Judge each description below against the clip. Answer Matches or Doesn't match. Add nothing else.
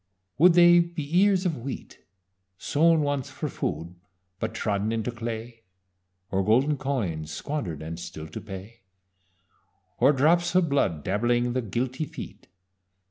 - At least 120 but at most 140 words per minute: Matches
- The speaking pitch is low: Matches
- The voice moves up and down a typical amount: Doesn't match